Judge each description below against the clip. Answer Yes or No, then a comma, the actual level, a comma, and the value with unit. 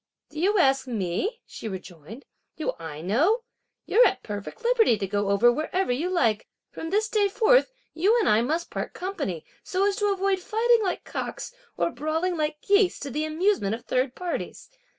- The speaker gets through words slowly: No, average, 185 wpm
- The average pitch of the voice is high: Yes, very high, 320 Hz